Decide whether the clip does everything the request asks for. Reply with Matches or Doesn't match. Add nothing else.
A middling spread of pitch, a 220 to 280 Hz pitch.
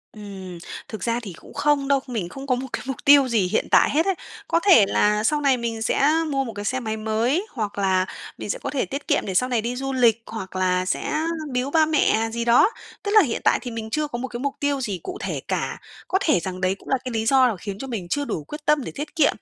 Matches